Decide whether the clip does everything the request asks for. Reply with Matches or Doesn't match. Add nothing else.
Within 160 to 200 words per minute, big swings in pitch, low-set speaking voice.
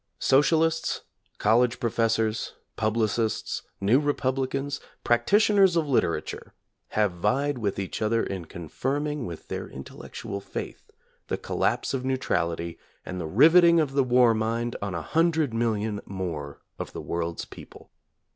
Doesn't match